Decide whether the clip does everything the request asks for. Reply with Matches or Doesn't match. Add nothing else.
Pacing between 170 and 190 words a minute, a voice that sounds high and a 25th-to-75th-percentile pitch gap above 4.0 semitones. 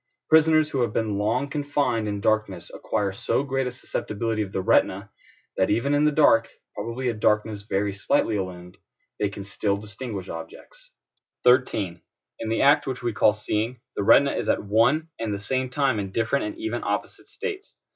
Doesn't match